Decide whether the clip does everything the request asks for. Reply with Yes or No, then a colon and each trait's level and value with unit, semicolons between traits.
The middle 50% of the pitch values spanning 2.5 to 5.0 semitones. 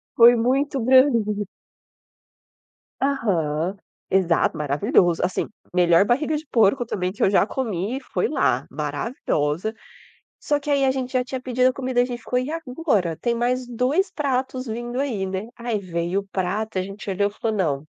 No: wide, 5.4 semitones